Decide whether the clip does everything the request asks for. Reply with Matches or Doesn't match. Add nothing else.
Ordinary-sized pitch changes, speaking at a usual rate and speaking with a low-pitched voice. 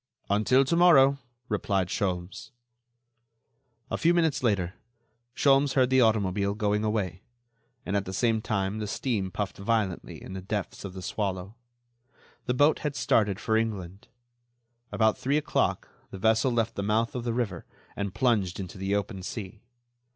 Matches